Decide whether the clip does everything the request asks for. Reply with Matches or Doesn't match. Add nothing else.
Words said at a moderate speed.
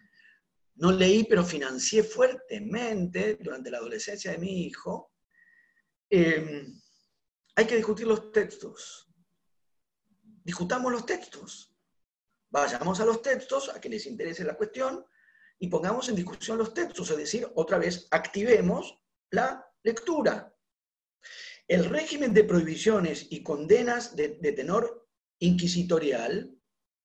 Doesn't match